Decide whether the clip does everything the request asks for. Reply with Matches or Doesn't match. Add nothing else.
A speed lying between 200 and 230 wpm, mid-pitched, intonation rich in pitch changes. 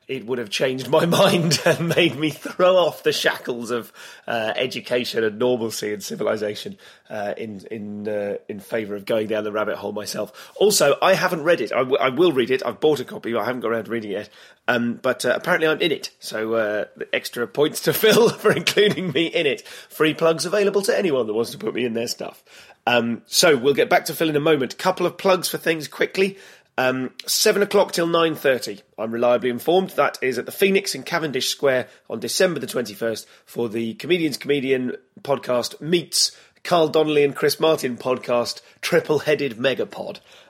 Matches